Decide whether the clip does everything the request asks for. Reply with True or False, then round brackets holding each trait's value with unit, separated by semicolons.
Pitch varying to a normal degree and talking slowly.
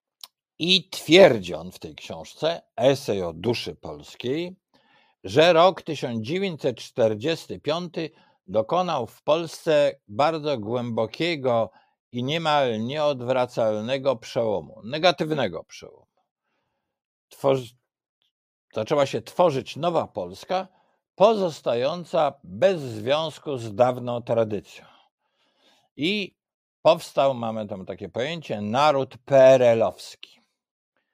False (6.1 semitones; 85 wpm)